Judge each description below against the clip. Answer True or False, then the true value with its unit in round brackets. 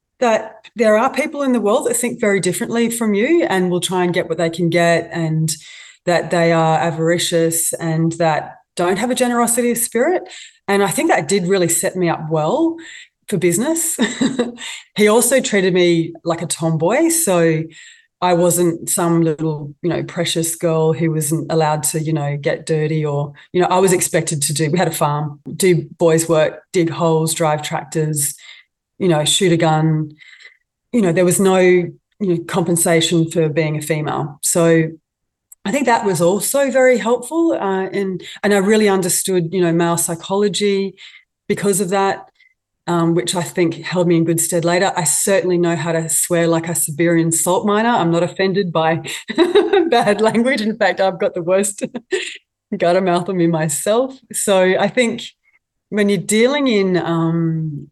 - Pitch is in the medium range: True (175 Hz)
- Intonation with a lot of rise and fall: False (3.9 semitones)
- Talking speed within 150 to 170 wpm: False (180 wpm)